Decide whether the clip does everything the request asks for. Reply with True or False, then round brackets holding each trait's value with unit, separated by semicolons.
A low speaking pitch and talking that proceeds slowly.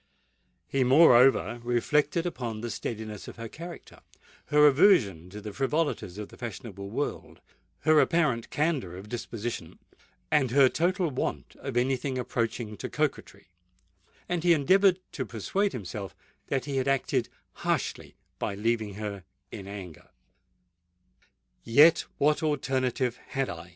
True (125 Hz; 125 wpm)